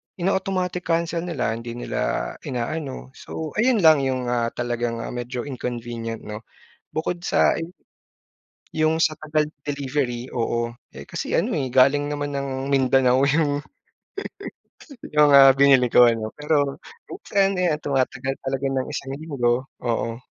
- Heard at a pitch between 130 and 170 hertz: Yes, low, 135 Hz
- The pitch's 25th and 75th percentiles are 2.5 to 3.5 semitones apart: No, average, 4.0 semitones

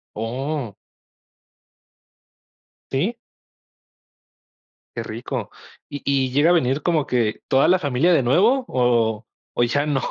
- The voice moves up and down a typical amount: Yes, average, 4.2 semitones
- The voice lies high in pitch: No, low, 135 Hz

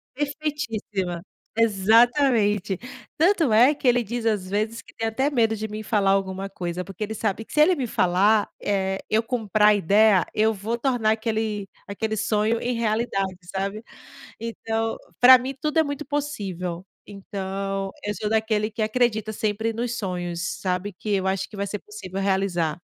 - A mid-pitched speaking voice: No, high, 215 Hz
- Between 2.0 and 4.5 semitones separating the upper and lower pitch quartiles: Yes, average, 2.9 semitones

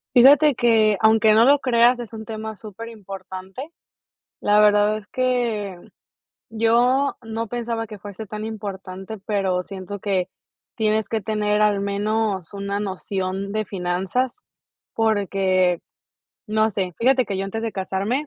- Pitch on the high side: Yes, high, 215 Hz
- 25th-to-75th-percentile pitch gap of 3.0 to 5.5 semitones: No, narrow, 2.5 semitones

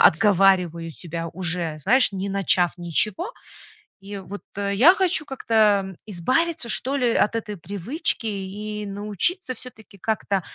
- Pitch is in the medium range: No, high, 200 Hz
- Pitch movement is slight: No, average, 3.6 semitones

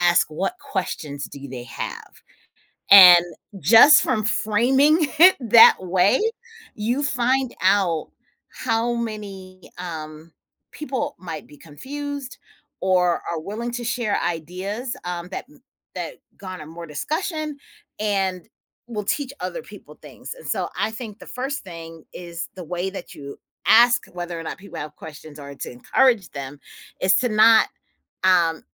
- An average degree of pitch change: No, wide, 6.2 semitones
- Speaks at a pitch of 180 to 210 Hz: Yes, high, 190 Hz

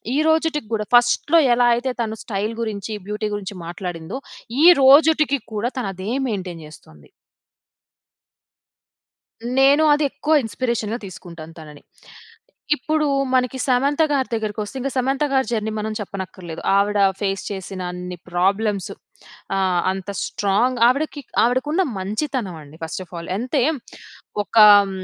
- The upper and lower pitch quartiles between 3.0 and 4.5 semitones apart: No, wide, 5.5 semitones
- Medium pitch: No, high, 215 Hz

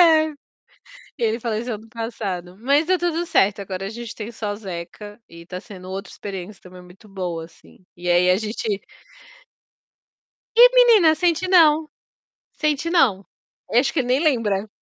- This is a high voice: Yes, high, 220 Hz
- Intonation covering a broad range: Yes, wide, 8.1 semitones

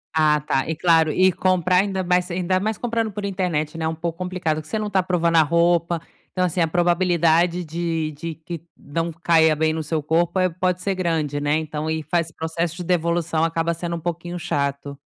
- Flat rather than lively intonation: Yes, narrow, 2.1 semitones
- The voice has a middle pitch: Yes, medium, 170 Hz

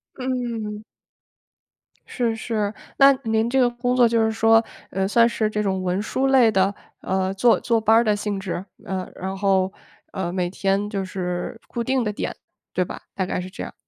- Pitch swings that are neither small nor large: Yes, average, 3.5 semitones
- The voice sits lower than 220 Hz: Yes, high, 210 Hz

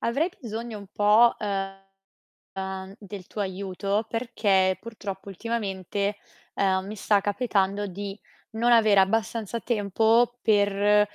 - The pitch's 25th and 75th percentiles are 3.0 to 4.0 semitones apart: No, narrow, 2.5 semitones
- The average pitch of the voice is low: No, high, 205 Hz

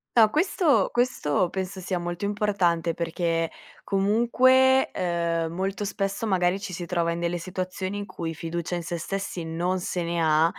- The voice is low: No, medium, 180 Hz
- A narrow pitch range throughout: No, average, 3.1 semitones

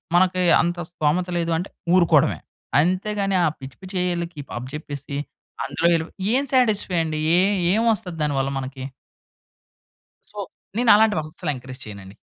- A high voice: No, medium, 170 Hz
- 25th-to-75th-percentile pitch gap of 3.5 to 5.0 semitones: Yes, average, 4.5 semitones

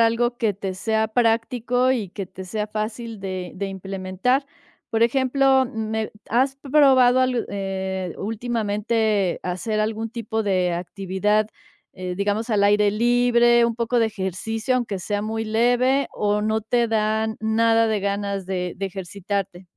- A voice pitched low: No, high, 220 Hz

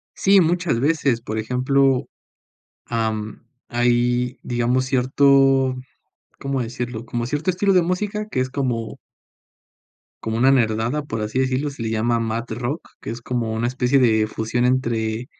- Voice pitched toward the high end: No, low, 125 Hz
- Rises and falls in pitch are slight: No, average, 3.0 semitones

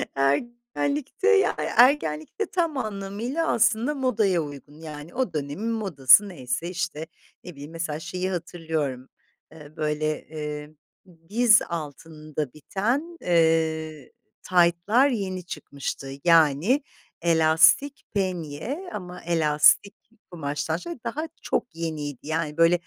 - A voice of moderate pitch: Yes, medium, 170 Hz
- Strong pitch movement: Yes, wide, 6.7 semitones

